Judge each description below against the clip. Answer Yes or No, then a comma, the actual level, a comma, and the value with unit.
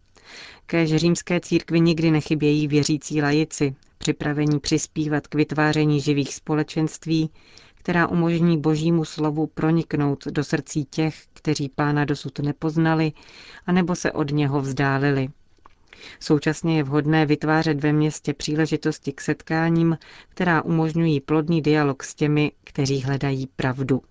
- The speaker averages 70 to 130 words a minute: Yes, average, 120 wpm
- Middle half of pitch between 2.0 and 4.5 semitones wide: No, narrow, 1.5 semitones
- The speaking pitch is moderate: Yes, medium, 155 Hz